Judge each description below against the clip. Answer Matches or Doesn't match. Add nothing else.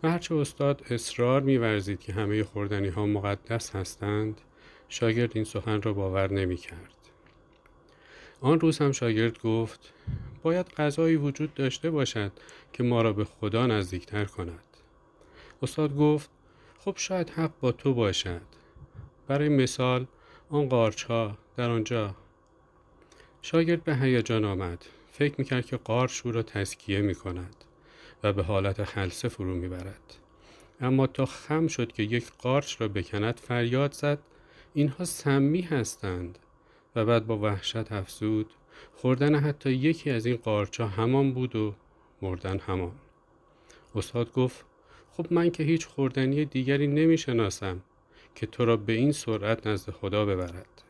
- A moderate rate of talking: Matches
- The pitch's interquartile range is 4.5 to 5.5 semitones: Matches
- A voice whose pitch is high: Doesn't match